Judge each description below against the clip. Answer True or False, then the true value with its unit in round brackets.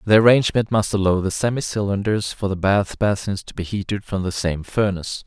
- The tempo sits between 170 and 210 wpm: True (205 wpm)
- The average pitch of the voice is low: True (100 Hz)